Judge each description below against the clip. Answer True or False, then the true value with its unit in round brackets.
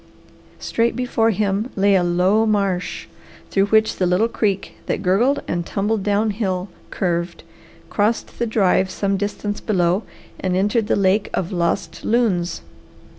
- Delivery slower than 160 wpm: True (145 wpm)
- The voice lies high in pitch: True (200 Hz)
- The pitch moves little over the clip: False (3.0 semitones)